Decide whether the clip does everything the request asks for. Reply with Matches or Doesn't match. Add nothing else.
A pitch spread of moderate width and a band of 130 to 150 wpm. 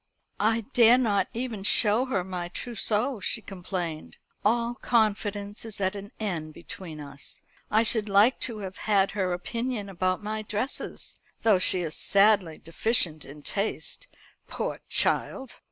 Matches